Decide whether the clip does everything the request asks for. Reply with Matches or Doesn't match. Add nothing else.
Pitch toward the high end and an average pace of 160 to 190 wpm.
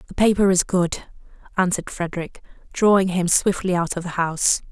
Doesn't match